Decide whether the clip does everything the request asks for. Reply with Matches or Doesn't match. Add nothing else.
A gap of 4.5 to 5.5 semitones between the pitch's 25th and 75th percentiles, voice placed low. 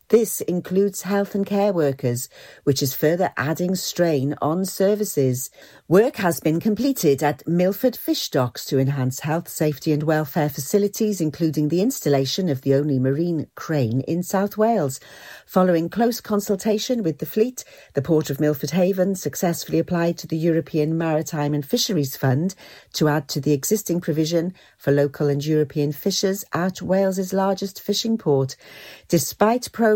Doesn't match